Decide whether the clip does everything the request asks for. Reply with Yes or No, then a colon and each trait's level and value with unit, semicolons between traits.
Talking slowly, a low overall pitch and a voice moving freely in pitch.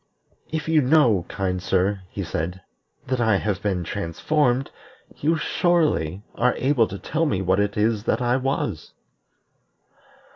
No: average, 145 wpm; low, 110 Hz; wide, 6.4 semitones